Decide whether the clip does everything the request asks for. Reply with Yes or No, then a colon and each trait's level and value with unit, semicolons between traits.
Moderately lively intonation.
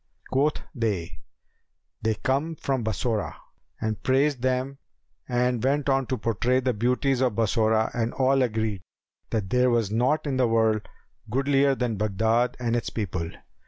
Yes: average, 3.1 semitones